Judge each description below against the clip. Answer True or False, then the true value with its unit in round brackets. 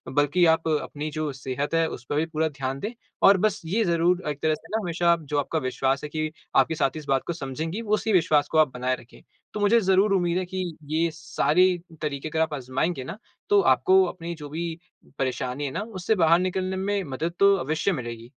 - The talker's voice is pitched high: False (160 Hz)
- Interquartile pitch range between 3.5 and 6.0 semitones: True (4.6 semitones)